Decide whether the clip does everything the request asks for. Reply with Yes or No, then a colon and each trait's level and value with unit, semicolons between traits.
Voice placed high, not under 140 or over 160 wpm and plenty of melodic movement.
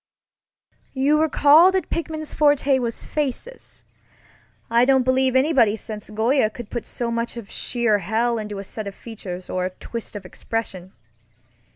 No: high, 235 Hz; average, 155 wpm; average, 4.3 semitones